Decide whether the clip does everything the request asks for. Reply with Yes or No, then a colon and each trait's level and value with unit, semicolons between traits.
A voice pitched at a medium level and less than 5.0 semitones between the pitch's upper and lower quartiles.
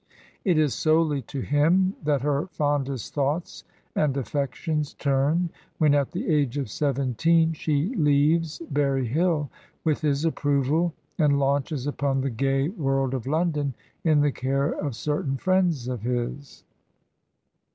Yes: medium, 145 Hz; narrow, 2.5 semitones